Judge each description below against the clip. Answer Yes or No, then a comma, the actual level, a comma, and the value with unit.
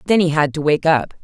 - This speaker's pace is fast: Yes, fast, 290 wpm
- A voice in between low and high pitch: Yes, medium, 160 Hz